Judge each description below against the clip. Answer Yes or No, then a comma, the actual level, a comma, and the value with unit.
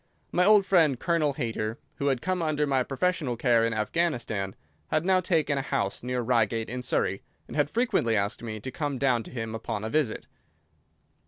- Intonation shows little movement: No, wide, 5.5 semitones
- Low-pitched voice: Yes, low, 130 Hz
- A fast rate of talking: No, average, 190 wpm